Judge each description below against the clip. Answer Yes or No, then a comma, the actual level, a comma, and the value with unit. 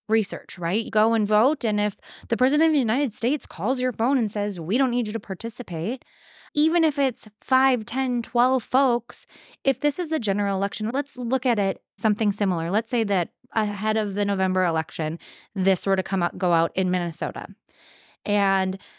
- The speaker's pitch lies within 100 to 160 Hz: No, high, 220 Hz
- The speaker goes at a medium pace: Yes, average, 195 wpm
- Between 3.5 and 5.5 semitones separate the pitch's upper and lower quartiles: Yes, average, 4.8 semitones